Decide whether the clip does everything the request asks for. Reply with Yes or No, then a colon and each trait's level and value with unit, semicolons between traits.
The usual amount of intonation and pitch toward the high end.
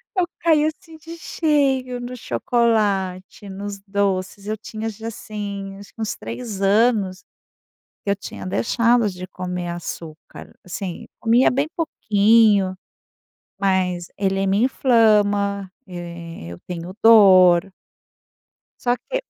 Yes: average, 3.8 semitones; high, 200 Hz